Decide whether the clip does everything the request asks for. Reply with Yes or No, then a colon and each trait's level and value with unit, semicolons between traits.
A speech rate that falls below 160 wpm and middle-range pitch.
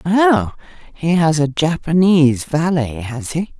Yes: slow, 135 wpm; medium, 160 Hz